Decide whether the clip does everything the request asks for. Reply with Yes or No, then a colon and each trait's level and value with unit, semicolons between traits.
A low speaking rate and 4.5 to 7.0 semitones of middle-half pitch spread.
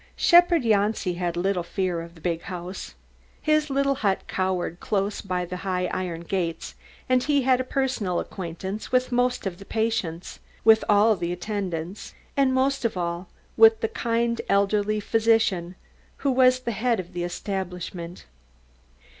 No: average, 160 wpm; wide, 5.6 semitones